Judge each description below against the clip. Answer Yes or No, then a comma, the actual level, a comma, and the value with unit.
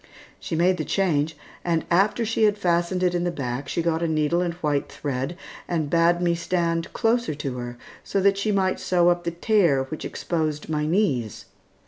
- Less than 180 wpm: No, average, 195 wpm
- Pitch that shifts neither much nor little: Yes, average, 3.2 semitones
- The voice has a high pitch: No, medium, 170 Hz